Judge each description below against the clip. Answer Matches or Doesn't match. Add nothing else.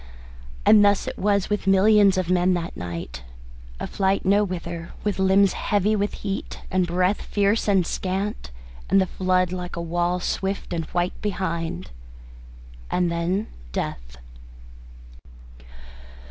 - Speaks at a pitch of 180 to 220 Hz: Matches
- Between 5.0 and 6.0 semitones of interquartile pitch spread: Doesn't match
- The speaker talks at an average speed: Doesn't match